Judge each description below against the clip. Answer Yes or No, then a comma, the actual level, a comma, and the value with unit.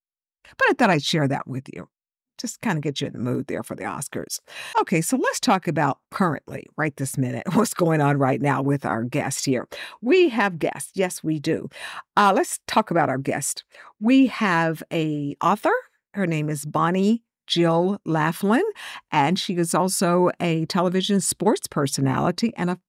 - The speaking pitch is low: No, medium, 170 Hz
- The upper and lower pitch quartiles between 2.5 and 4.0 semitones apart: No, average, 5.2 semitones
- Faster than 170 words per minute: Yes, average, 185 wpm